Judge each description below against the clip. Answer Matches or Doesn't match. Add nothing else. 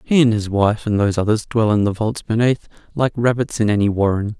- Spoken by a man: Matches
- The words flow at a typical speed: Doesn't match